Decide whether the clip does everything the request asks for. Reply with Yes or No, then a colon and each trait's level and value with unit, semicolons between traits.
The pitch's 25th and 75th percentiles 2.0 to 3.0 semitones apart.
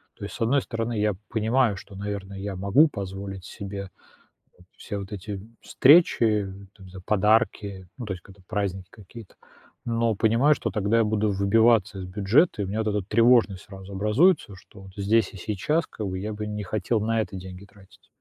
Yes: average, 2.7 semitones